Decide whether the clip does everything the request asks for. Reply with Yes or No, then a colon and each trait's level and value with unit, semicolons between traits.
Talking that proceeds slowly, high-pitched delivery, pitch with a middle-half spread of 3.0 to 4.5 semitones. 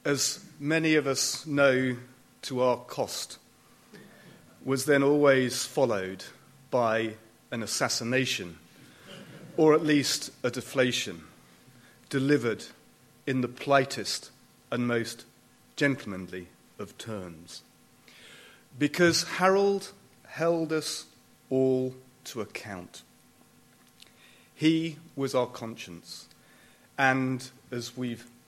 No: slow, 90 wpm; low, 130 Hz; average, 3.4 semitones